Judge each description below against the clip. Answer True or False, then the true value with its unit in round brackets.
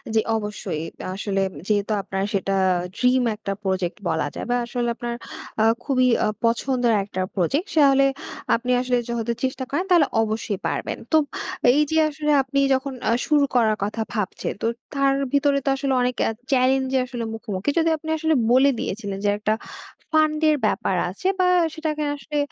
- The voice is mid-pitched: False (250 Hz)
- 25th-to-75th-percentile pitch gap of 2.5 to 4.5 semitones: False (5.0 semitones)